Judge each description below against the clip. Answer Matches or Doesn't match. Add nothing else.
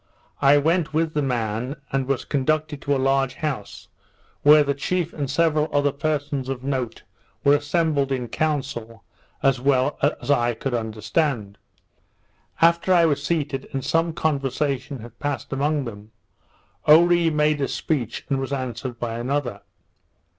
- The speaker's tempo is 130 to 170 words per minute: Matches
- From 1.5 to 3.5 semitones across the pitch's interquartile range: Matches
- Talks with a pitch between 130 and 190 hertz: Matches